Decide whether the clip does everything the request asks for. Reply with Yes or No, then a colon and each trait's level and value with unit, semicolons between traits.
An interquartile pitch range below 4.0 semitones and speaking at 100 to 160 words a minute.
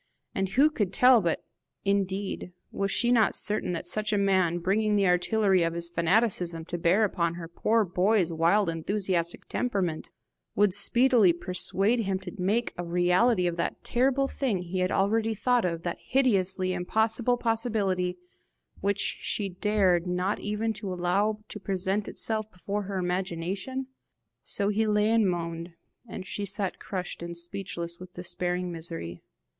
Yes: average, 3.2 semitones; average, 155 wpm